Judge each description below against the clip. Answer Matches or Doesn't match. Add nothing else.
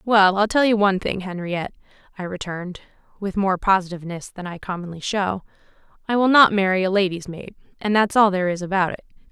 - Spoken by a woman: Matches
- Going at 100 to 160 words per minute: Doesn't match